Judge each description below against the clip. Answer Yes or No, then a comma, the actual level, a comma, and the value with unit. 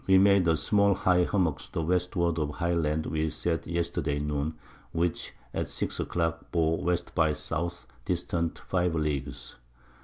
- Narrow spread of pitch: Yes, narrow, 2.2 semitones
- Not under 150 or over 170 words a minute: No, average, 180 wpm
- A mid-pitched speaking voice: No, very low, 85 Hz